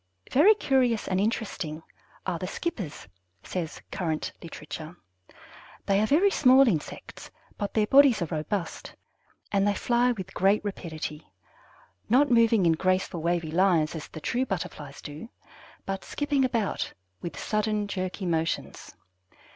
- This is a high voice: Yes, high, 195 Hz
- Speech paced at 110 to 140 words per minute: Yes, slow, 135 wpm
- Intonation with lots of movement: Yes, wide, 6.1 semitones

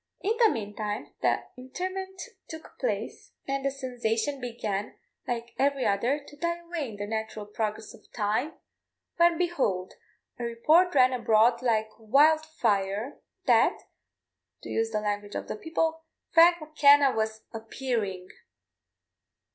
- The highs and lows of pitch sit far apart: Yes, wide, 6.4 semitones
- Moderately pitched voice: No, high, 245 Hz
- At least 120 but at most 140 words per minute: Yes, slow, 135 wpm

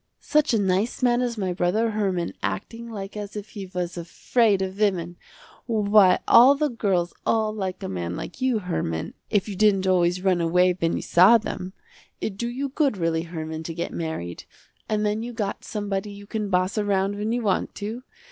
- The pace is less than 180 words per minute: No, average, 195 wpm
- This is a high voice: Yes, high, 200 Hz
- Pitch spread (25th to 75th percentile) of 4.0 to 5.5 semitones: No, average, 3.5 semitones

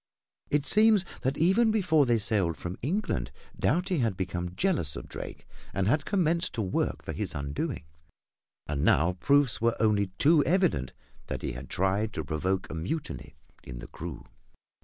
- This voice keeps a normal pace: Yes, average, 165 wpm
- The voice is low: Yes, low, 115 Hz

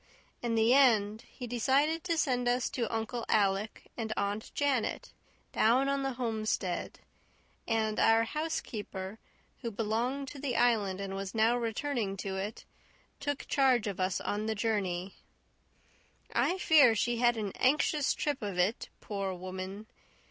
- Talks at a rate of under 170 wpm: Yes, average, 150 wpm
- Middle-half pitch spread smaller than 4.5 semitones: Yes, average, 4.0 semitones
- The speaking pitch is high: Yes, high, 225 Hz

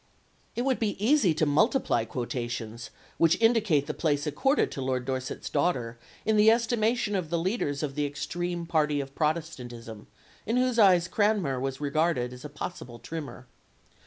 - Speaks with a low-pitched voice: No, medium, 155 Hz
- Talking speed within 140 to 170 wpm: Yes, average, 165 wpm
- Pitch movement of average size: No, wide, 7.6 semitones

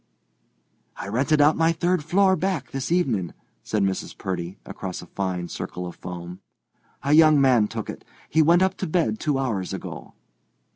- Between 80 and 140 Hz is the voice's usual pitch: Yes, low, 135 Hz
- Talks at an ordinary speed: Yes, average, 175 wpm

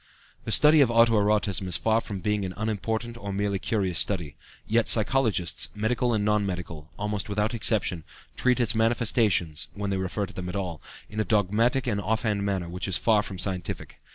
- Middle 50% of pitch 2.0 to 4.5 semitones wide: Yes, average, 2.9 semitones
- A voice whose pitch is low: Yes, low, 105 Hz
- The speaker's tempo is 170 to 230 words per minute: Yes, average, 195 wpm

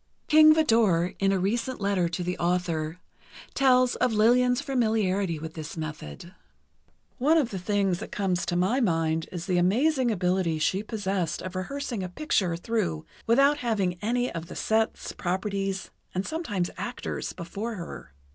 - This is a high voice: Yes, high, 195 Hz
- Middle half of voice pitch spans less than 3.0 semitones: No, average, 5.0 semitones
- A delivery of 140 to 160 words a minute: Yes, average, 155 wpm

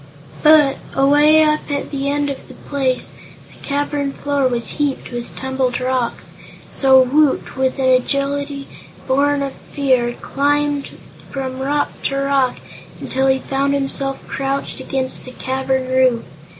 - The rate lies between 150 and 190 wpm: No, average, 140 wpm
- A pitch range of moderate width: No, narrow, 1.5 semitones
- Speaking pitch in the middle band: No, very high, 275 Hz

